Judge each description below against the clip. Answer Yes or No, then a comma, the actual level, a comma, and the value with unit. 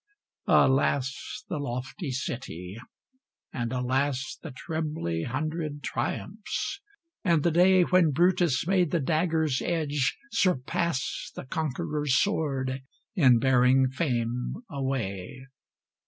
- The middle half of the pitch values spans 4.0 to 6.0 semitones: Yes, average, 4.5 semitones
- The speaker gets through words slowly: Yes, slow, 100 wpm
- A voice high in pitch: No, medium, 140 Hz